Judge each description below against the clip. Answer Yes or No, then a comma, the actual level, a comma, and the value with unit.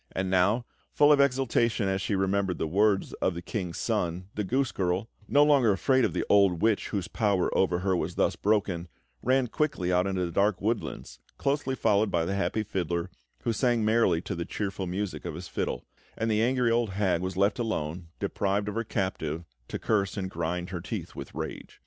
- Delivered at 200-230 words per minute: Yes, fast, 205 wpm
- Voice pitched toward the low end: Yes, low, 100 Hz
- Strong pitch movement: No, average, 3.9 semitones